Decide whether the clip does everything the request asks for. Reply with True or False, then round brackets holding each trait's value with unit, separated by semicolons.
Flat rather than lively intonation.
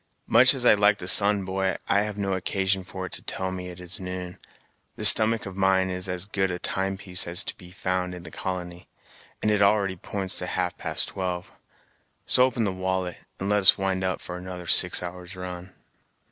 True (1.6 semitones)